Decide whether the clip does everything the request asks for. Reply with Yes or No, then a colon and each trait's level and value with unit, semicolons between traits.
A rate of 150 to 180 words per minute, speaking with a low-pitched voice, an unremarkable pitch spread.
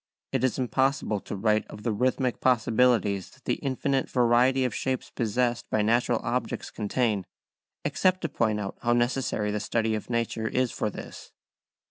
Yes: average, 165 wpm; low, 120 Hz; average, 3.0 semitones